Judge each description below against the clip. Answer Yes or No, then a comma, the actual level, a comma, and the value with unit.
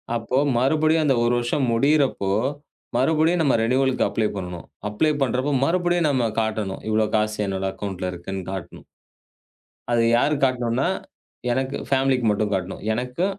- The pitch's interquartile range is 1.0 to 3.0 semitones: No, average, 4.7 semitones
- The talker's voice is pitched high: No, low, 125 Hz